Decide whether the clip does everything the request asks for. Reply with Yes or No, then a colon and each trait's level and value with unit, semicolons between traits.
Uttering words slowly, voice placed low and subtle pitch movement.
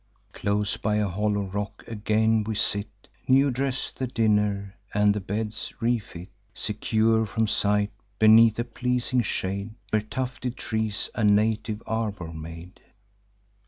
Yes: slow, 130 wpm; low, 105 Hz; narrow, 1.8 semitones